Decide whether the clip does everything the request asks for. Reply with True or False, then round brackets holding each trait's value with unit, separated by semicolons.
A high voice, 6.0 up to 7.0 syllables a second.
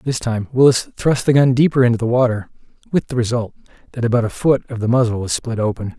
False (120 Hz; 6.1 syllables/s)